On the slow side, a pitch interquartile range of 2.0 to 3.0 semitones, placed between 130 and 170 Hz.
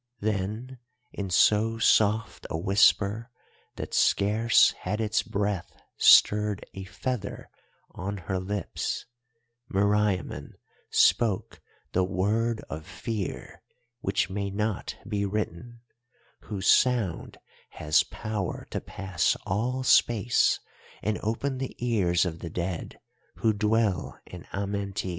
No: slow, 110 wpm; narrow, 2.6 semitones; low, 105 Hz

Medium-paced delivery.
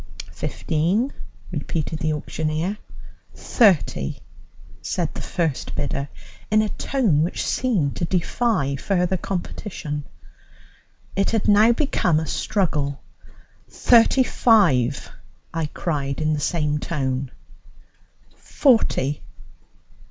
No: slow, 100 wpm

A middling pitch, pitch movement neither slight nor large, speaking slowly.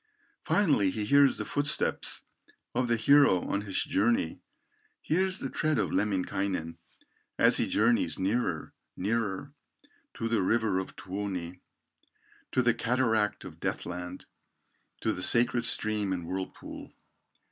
No: low, 105 Hz; average, 4.4 semitones; slow, 130 wpm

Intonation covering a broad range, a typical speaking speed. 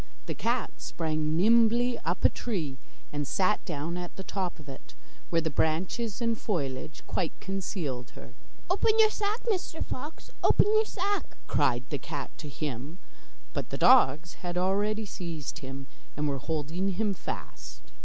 Yes: wide, 6.7 semitones; average, 160 wpm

